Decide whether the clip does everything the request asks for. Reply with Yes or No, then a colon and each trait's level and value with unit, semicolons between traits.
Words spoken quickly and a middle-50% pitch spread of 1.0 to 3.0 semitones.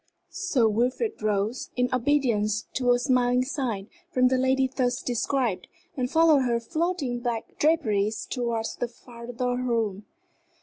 No: slow, 135 wpm; narrow, 2.4 semitones